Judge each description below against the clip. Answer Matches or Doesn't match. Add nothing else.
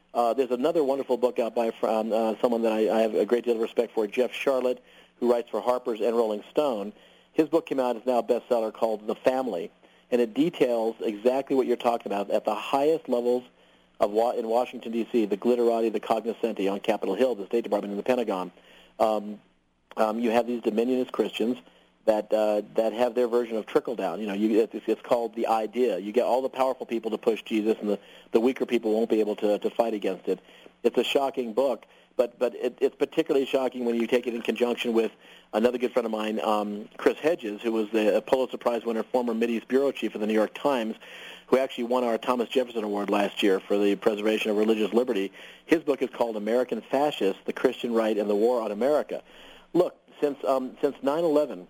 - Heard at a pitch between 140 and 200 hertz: Doesn't match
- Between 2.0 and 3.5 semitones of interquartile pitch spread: Matches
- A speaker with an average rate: Doesn't match